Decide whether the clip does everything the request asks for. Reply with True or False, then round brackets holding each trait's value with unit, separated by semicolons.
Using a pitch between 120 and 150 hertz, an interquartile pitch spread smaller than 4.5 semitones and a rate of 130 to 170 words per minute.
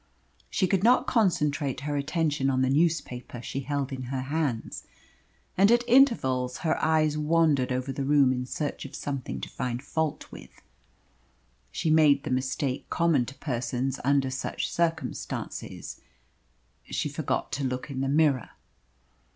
True (140 Hz; 3.5 semitones; 150 wpm)